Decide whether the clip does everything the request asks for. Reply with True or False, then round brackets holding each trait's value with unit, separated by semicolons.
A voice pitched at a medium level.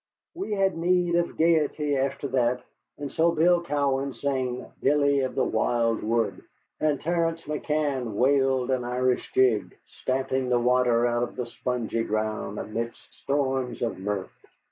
False (130 Hz)